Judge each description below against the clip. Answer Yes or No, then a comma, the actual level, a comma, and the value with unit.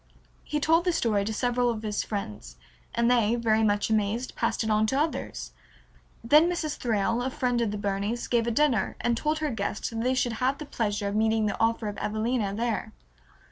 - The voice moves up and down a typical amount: Yes, average, 3.0 semitones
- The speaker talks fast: Yes, fast, 210 wpm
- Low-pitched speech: No, high, 230 Hz